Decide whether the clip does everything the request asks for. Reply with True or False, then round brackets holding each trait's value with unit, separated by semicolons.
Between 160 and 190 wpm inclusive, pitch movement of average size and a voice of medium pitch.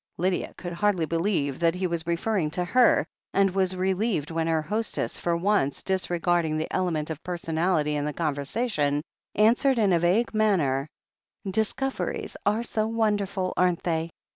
True (165 wpm; 4.3 semitones; 180 Hz)